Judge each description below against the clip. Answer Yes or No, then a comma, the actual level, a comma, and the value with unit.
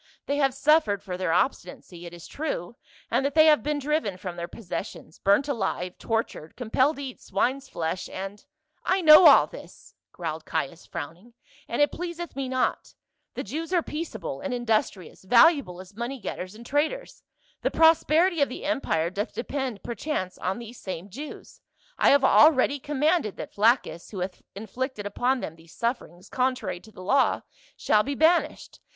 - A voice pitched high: Yes, high, 245 Hz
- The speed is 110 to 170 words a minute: No, average, 180 wpm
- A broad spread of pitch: Yes, wide, 7.7 semitones